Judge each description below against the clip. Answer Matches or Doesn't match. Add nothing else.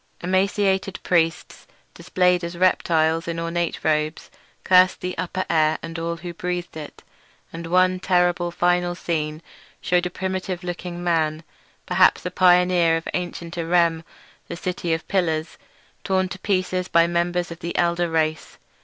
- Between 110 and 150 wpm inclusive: Matches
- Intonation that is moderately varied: Doesn't match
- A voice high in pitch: Doesn't match